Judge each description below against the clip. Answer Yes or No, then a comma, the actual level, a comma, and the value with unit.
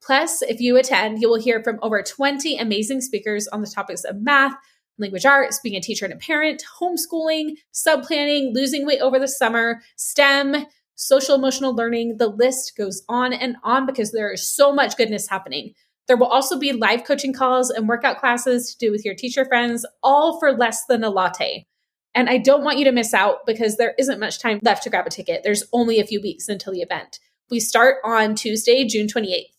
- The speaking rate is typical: No, fast, 210 wpm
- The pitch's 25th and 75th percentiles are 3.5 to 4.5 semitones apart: Yes, average, 3.8 semitones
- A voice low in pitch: No, very high, 250 Hz